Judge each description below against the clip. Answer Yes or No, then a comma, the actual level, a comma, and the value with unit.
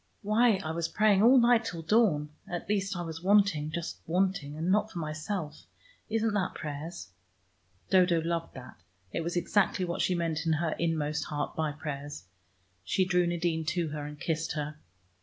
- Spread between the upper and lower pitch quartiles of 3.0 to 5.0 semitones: Yes, average, 3.7 semitones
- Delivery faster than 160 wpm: Yes, average, 175 wpm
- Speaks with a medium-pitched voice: Yes, medium, 170 Hz